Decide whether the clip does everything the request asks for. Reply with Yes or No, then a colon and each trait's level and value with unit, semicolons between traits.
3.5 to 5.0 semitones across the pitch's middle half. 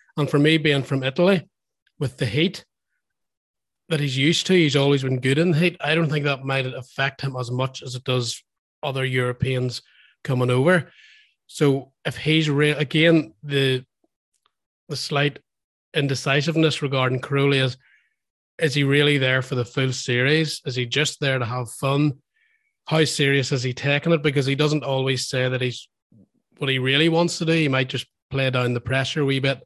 No: average, 2.9 semitones